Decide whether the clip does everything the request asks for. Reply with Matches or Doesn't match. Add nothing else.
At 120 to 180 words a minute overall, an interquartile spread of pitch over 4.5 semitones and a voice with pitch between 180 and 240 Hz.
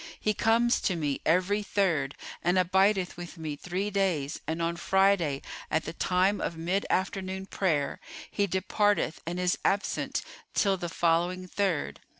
Doesn't match